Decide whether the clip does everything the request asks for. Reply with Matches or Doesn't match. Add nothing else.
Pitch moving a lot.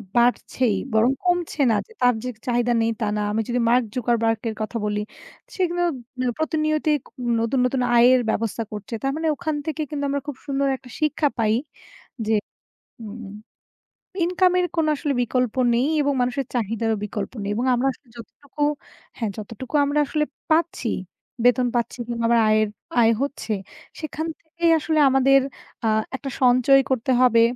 Doesn't match